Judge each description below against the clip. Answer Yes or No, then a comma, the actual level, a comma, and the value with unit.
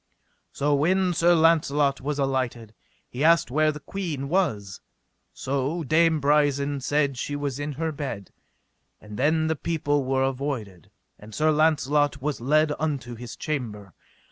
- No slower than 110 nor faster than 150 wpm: Yes, average, 145 wpm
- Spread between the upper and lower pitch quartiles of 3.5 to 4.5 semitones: No, average, 2.9 semitones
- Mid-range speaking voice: Yes, medium, 145 Hz